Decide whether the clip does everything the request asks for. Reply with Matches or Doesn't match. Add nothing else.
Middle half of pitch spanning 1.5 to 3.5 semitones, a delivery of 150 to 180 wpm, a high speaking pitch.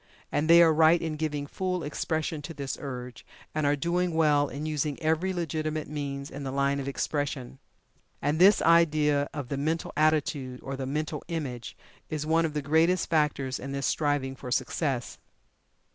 Doesn't match